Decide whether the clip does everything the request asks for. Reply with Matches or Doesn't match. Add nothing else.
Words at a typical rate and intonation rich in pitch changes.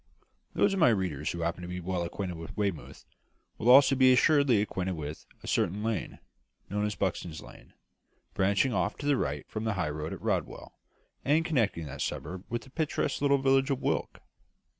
Matches